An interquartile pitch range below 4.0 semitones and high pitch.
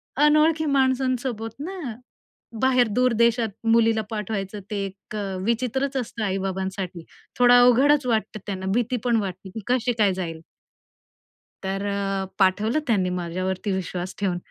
No: average, 4.6 semitones; high, 220 Hz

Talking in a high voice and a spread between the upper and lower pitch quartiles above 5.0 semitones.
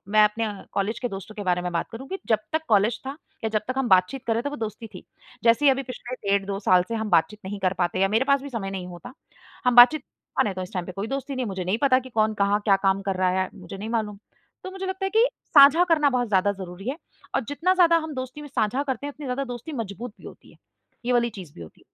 Yes: high, 225 Hz; wide, 5.4 semitones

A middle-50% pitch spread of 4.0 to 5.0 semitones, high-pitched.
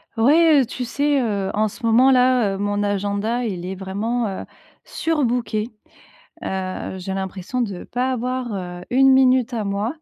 Yes: average, 4.3 semitones; high, 225 Hz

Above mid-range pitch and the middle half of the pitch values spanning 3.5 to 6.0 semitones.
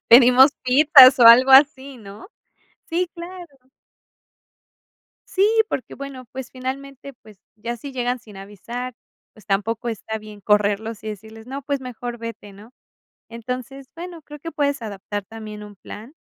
Yes: high, 245 Hz; average, 4.1 semitones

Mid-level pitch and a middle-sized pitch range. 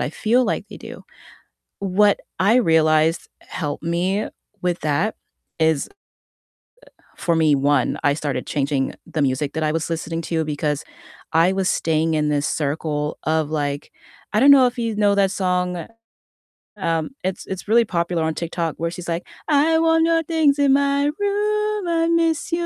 No: medium, 170 Hz; wide, 7.8 semitones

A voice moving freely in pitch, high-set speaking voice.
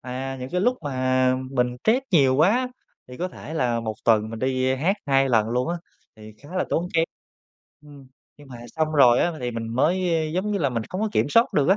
No: wide, 5.7 semitones; low, 135 Hz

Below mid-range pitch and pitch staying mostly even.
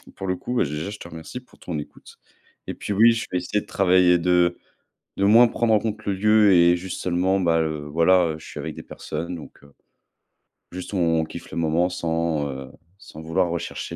No: very low, 90 Hz; average, 3.3 semitones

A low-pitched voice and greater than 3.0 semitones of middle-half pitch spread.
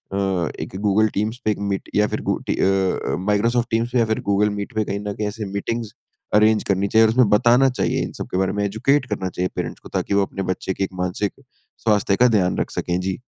No: low, 105 Hz; narrow, 2.4 semitones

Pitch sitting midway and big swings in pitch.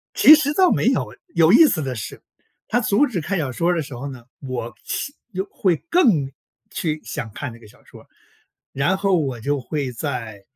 Yes: medium, 150 Hz; wide, 7.6 semitones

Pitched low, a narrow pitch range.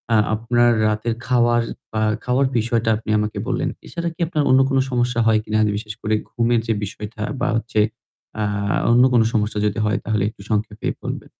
Yes: low, 115 Hz; narrow, 2.0 semitones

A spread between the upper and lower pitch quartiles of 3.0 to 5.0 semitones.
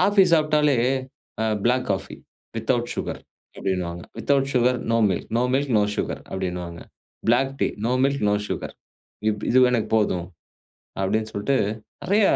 No: wide, 5.4 semitones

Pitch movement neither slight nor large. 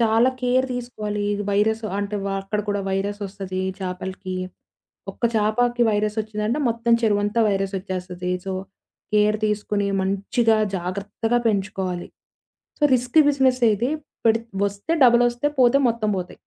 Yes: average, 3.2 semitones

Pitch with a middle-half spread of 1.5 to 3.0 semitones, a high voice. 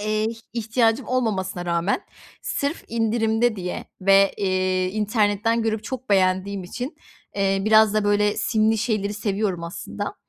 Yes: narrow, 2.4 semitones; high, 210 Hz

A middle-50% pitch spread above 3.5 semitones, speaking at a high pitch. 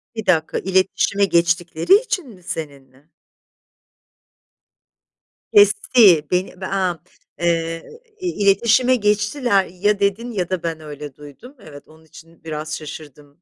No: average, 4.8 semitones; medium, 180 Hz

